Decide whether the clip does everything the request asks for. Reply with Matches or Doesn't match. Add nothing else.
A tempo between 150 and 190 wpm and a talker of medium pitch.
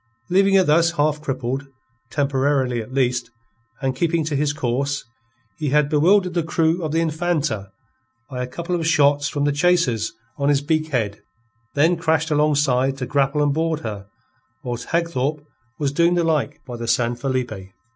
Matches